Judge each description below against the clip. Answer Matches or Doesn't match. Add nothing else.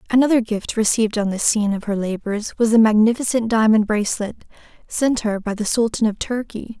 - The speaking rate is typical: Matches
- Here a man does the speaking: Doesn't match